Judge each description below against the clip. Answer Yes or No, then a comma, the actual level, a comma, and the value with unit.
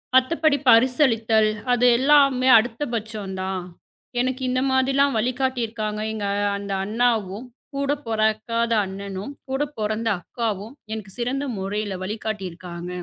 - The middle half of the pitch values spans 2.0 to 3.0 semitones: No, average, 3.8 semitones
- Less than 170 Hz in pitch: No, high, 225 Hz